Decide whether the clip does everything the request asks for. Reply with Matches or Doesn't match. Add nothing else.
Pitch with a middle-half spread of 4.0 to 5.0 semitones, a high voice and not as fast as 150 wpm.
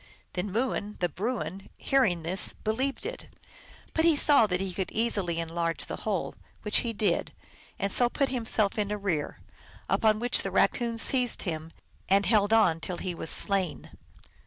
Doesn't match